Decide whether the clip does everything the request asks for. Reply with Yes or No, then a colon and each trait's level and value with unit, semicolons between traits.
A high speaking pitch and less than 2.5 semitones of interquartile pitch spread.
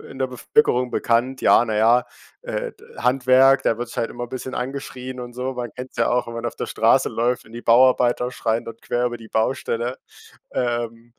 No: low, 125 Hz; narrow, 1.6 semitones